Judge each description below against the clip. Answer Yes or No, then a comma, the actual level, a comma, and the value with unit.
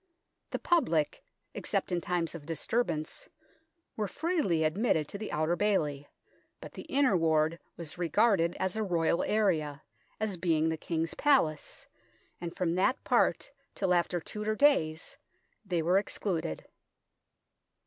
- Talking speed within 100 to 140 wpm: Yes, slow, 135 wpm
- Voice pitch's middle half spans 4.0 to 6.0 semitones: Yes, average, 4.8 semitones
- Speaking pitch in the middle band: Yes, medium, 175 Hz